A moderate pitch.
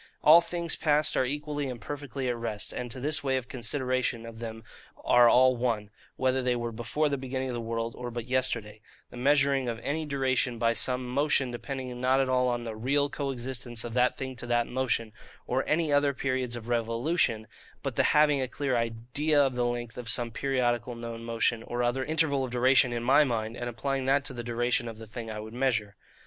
No: low, 125 Hz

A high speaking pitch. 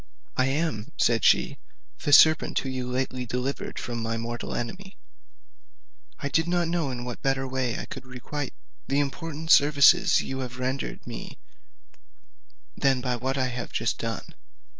No: low, 135 Hz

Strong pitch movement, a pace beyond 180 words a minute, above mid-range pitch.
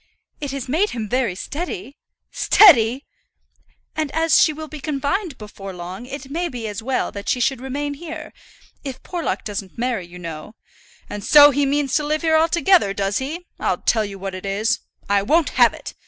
Yes: wide, 6.9 semitones; average, 195 wpm; very high, 270 Hz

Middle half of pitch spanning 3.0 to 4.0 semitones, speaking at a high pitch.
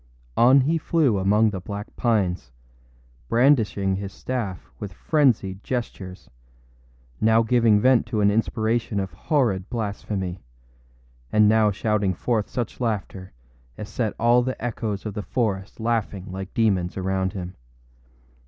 No: average, 3.5 semitones; low, 105 Hz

